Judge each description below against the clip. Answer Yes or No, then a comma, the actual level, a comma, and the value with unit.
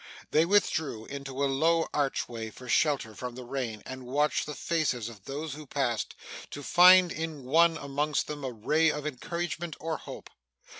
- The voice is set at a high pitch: No, medium, 145 Hz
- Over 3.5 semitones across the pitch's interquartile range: Yes, average, 3.9 semitones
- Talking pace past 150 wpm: Yes, average, 170 wpm